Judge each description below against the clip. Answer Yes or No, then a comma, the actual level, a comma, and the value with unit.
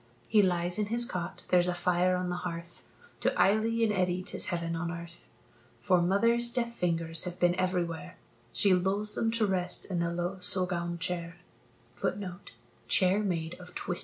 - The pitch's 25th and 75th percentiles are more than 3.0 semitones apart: No, average, 2.7 semitones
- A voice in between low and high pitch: Yes, medium, 180 Hz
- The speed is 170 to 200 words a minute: No, average, 155 wpm